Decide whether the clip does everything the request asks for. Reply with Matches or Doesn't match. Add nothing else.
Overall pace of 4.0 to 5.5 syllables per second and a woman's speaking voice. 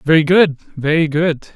Doesn't match